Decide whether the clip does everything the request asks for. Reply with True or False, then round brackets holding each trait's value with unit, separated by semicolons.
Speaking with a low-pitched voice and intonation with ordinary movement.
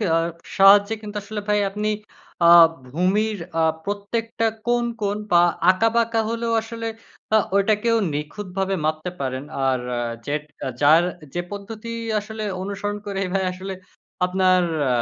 False (200 Hz; 3.1 semitones)